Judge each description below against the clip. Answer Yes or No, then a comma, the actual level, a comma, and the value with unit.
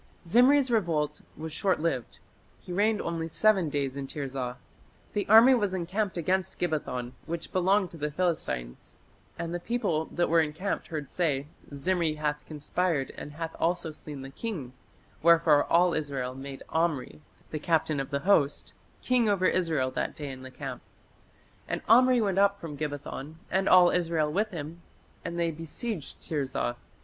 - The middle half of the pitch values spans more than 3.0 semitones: Yes, average, 4.2 semitones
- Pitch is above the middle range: No, medium, 165 Hz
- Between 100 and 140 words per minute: No, average, 160 wpm